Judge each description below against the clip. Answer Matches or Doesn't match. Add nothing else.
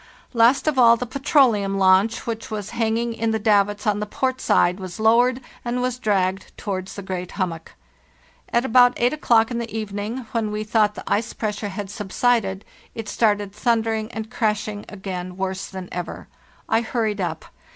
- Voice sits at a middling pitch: Doesn't match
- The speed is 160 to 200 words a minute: Matches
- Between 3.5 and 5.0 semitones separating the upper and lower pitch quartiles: Doesn't match